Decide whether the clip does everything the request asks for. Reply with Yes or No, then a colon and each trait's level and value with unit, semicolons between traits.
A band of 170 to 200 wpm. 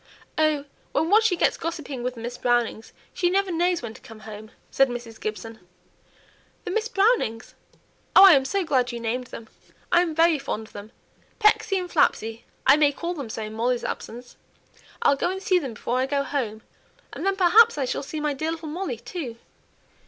Yes: average, 195 wpm